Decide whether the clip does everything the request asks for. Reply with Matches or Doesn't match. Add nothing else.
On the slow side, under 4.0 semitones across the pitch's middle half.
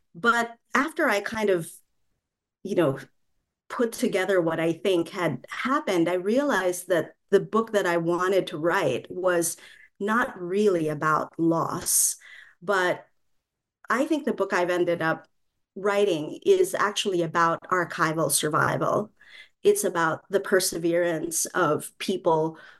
Doesn't match